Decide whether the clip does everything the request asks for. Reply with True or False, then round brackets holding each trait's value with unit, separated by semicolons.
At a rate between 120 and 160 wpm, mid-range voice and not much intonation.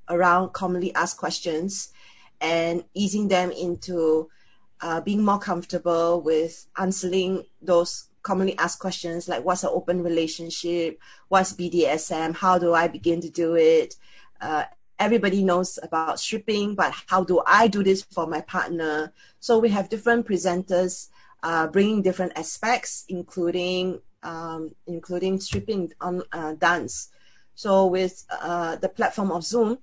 True (140 wpm; 180 Hz; 2.3 semitones)